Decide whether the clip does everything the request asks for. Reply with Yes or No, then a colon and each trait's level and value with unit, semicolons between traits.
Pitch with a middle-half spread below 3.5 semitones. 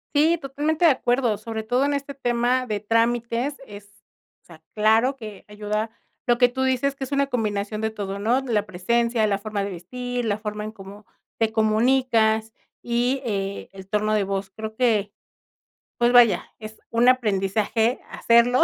Yes: average, 3.0 semitones